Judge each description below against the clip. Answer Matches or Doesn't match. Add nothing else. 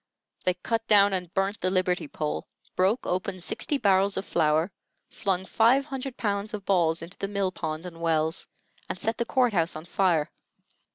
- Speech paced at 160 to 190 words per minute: Matches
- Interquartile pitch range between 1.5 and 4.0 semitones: Matches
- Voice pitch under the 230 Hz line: Matches